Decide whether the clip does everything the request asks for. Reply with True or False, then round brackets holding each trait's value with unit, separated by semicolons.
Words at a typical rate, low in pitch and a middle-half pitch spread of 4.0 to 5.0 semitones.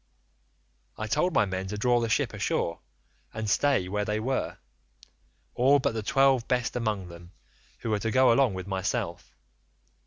True (165 wpm; 110 Hz; 4.3 semitones)